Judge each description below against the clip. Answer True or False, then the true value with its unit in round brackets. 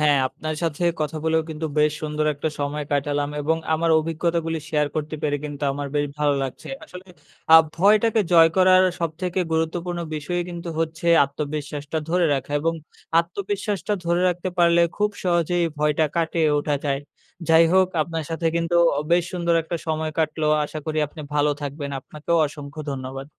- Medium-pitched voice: True (160 Hz)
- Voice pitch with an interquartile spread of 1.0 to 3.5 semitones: True (2.6 semitones)